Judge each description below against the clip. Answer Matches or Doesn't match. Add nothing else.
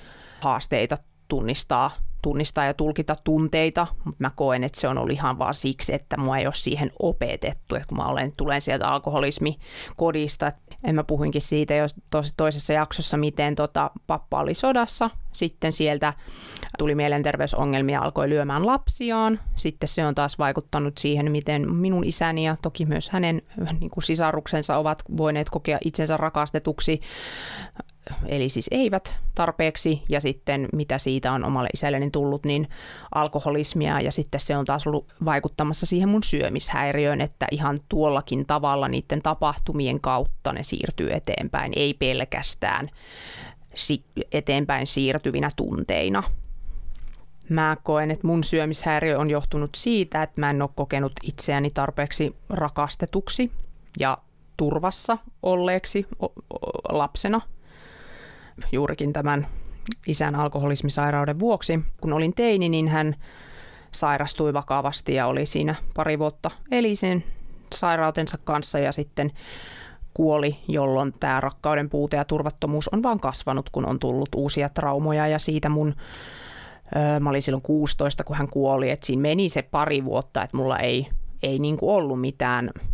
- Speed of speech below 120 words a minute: Doesn't match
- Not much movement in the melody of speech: Matches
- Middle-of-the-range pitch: Matches